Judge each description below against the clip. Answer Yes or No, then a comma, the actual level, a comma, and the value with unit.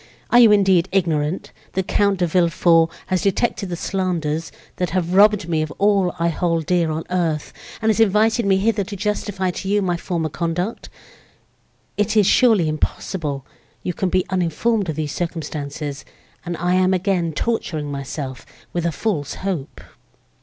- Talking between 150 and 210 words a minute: Yes, average, 165 wpm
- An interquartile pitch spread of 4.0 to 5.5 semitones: No, average, 3.4 semitones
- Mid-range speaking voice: Yes, medium, 180 Hz